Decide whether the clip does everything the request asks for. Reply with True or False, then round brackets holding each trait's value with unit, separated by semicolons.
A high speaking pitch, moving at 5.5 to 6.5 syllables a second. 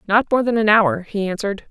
True (210 Hz; 6.0 syllables/s)